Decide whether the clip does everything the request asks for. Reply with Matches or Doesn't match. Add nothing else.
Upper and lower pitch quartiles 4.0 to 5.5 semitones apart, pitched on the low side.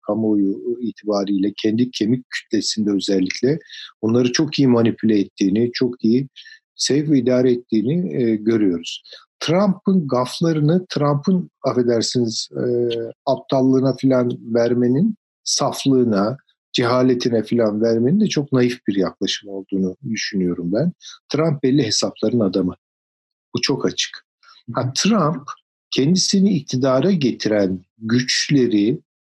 Matches